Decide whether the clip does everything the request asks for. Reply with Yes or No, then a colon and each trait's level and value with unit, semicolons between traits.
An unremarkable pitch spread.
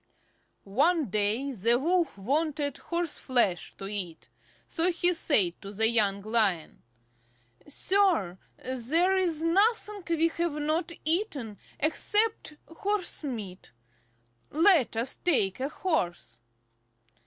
No: wide, 8.4 semitones